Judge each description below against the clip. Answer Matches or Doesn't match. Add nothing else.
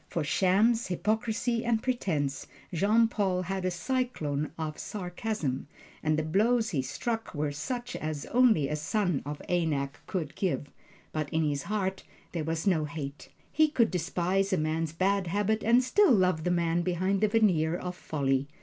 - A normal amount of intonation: Doesn't match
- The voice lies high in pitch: Doesn't match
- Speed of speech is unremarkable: Matches